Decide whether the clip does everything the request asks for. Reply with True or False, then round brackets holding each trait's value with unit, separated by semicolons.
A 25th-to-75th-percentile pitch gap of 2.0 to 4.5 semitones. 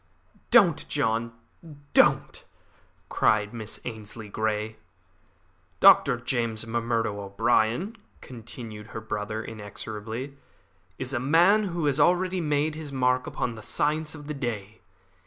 False (4.9 semitones)